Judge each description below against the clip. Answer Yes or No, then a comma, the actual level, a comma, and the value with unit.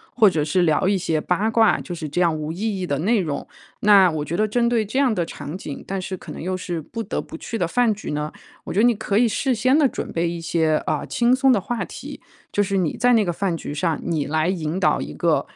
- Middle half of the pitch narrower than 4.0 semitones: No, average, 5.2 semitones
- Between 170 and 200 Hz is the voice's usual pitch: Yes, high, 190 Hz